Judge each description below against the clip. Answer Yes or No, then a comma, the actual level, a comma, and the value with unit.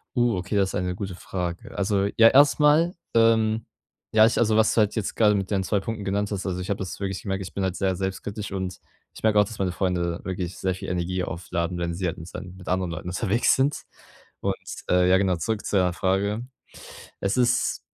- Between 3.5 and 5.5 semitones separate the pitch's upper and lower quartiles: No, average, 2.9 semitones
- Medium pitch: No, very low, 95 Hz